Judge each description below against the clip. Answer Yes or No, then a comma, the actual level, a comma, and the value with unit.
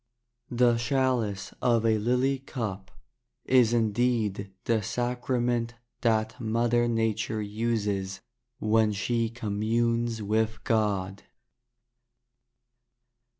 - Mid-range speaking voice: No, low, 115 Hz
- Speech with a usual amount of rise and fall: No, narrow, 2.0 semitones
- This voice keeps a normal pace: No, slow, 85 wpm